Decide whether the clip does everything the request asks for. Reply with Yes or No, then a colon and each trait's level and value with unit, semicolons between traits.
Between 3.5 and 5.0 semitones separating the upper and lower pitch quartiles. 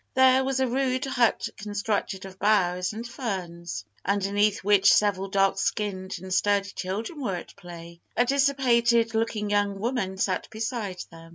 Yes: average, 3.8 semitones